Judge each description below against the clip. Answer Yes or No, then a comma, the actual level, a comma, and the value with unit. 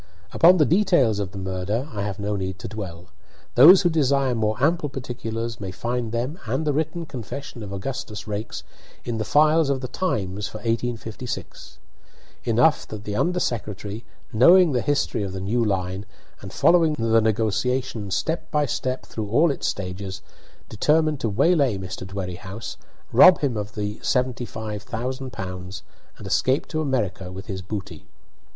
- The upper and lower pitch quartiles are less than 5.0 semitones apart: No, wide, 5.4 semitones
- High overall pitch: No, low, 115 Hz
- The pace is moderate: Yes, average, 165 wpm